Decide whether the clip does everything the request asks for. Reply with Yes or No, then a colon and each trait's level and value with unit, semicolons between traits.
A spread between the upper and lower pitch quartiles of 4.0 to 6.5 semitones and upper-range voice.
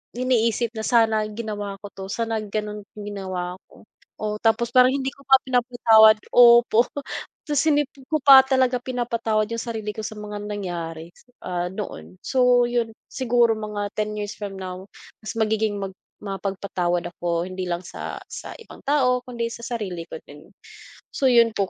No: average, 3.4 semitones; high, 220 Hz